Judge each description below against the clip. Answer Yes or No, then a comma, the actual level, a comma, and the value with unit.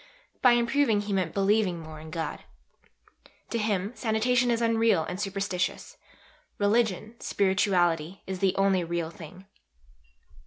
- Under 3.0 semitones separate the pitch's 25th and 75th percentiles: No, average, 3.8 semitones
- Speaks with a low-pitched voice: No, high, 195 Hz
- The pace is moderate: No, slow, 125 wpm